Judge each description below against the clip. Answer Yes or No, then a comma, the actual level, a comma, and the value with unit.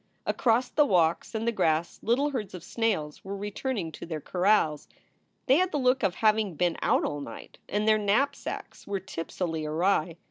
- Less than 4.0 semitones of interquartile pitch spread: No, wide, 5.6 semitones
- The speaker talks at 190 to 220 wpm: No, average, 180 wpm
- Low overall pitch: No, high, 200 Hz